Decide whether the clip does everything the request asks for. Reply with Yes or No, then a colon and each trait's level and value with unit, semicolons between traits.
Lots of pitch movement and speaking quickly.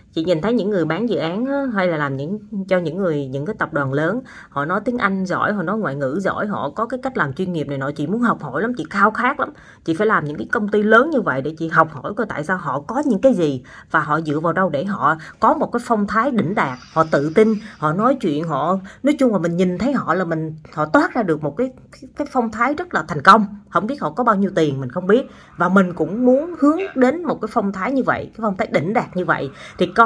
Yes: wide, 6.8 semitones; fast, 290 wpm